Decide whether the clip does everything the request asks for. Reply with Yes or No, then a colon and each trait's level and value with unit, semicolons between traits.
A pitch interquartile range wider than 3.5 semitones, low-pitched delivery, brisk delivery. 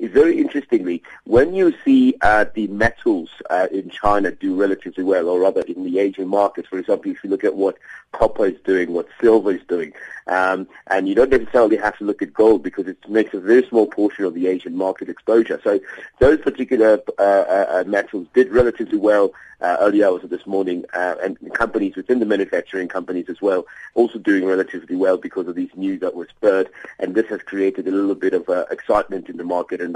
Yes: average, 4.9 semitones; low, 105 Hz; fast, 210 wpm